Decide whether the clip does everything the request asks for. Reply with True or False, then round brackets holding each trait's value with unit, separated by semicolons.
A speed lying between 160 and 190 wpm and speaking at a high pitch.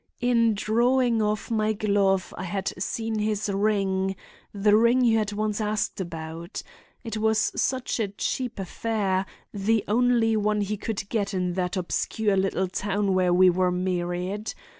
False (150 wpm; 205 Hz)